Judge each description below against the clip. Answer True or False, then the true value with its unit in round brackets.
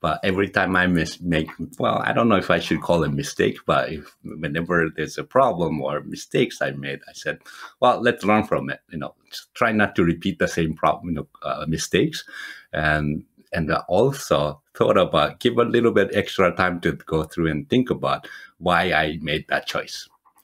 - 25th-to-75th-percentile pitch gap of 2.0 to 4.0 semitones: True (3.3 semitones)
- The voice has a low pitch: True (80 Hz)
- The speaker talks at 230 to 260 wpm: False (200 wpm)